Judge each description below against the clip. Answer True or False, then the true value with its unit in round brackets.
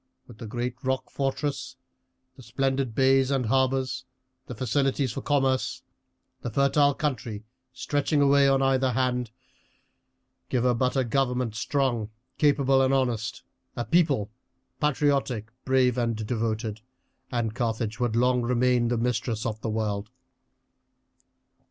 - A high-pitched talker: False (125 Hz)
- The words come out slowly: True (130 wpm)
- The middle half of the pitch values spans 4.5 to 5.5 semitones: False (2.6 semitones)